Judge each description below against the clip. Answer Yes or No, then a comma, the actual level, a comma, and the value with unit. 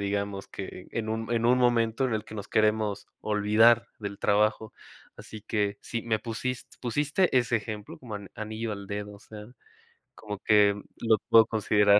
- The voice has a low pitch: Yes, low, 110 Hz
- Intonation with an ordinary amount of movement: No, narrow, 1.9 semitones